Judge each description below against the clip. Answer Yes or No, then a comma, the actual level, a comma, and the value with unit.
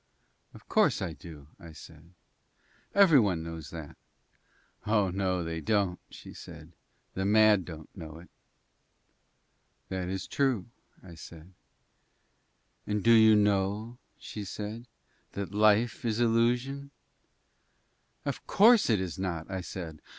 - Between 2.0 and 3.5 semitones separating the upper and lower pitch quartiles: No, average, 4.5 semitones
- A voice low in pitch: Yes, very low, 95 Hz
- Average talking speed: No, slow, 130 wpm